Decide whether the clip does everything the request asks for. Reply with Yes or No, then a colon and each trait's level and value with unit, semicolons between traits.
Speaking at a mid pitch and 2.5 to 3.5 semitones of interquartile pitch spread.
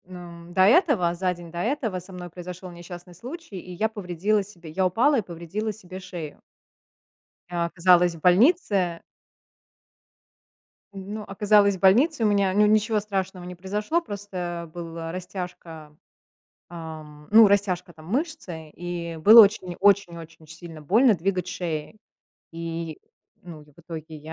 Yes: medium, 180 Hz; average, 3.2 semitones